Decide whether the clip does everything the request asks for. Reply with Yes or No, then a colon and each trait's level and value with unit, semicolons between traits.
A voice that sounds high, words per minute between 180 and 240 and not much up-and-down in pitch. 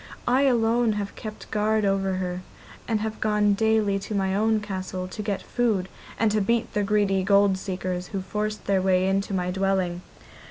Yes: high, 200 Hz; average, 185 wpm; narrow, 2.2 semitones